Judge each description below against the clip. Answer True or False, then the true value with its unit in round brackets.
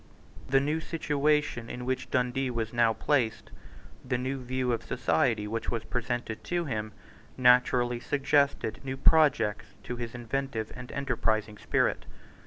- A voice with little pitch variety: False (3.1 semitones)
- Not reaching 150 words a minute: True (140 wpm)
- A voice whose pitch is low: True (125 Hz)